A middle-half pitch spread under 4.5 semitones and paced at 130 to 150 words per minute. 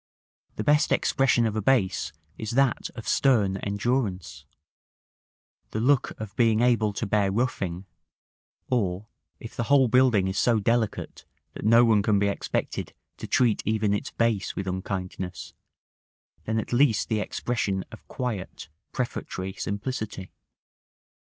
Yes: average, 3.5 semitones; average, 140 wpm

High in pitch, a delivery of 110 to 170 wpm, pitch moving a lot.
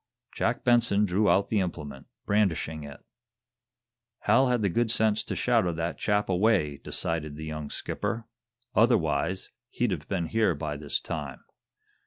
No: very low, 90 Hz; average, 150 wpm; wide, 5.9 semitones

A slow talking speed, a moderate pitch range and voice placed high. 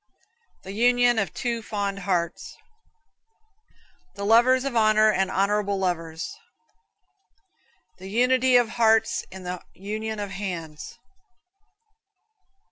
Yes: slow, 105 wpm; average, 3.4 semitones; high, 205 Hz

